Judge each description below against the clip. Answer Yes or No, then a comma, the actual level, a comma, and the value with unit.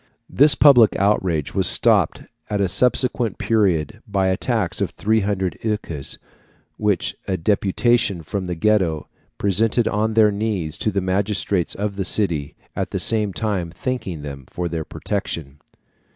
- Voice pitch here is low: Yes, low, 100 Hz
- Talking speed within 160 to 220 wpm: No, average, 150 wpm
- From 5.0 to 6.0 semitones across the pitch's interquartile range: No, average, 3.8 semitones